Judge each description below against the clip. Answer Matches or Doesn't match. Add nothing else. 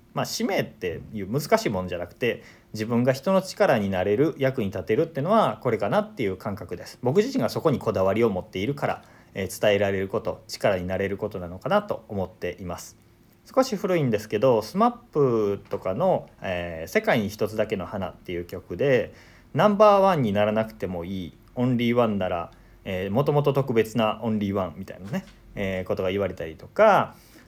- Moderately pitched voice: Doesn't match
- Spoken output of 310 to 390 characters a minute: Doesn't match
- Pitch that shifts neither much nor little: Doesn't match